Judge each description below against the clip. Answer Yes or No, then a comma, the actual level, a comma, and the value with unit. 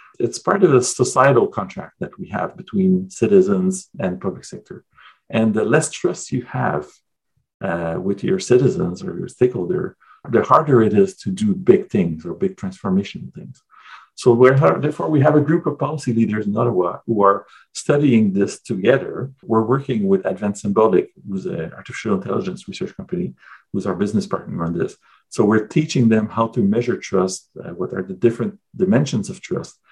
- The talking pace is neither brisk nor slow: Yes, average, 180 wpm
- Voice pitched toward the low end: Yes, low, 125 Hz